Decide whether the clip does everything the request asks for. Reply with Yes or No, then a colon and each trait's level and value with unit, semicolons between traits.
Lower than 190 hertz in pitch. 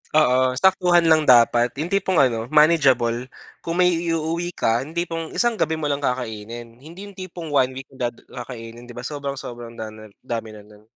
Yes: low, 135 Hz